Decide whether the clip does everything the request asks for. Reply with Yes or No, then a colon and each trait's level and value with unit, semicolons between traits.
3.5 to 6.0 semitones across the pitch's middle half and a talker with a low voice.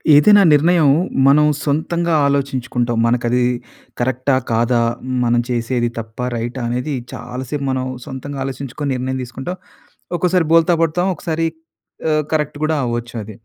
Yes: average, 4.0 semitones; low, 130 Hz